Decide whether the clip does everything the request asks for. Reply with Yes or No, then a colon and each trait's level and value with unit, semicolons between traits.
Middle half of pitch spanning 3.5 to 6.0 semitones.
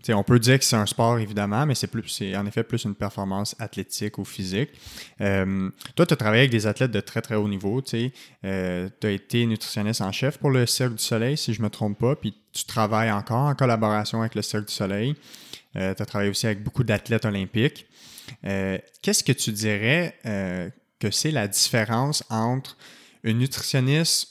Yes: average, 4.0 semitones